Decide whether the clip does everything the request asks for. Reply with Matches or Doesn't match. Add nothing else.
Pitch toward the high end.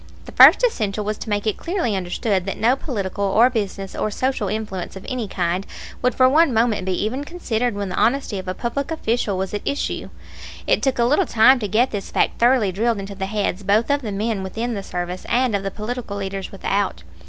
Matches